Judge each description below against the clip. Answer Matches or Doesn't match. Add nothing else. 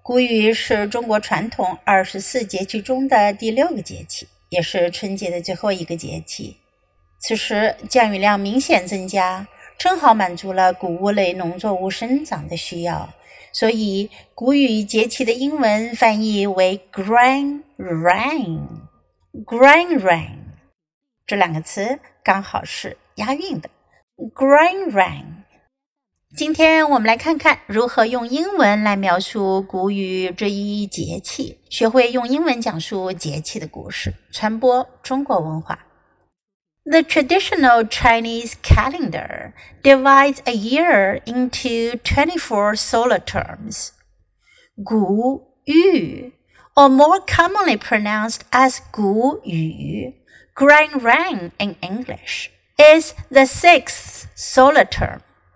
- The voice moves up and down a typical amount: Doesn't match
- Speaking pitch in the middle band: Doesn't match